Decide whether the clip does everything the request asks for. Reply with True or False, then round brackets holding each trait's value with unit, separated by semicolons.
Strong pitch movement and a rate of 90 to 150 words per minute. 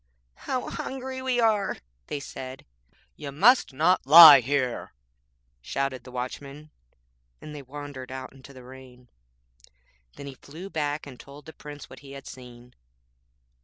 False (3.0 semitones; 145 wpm)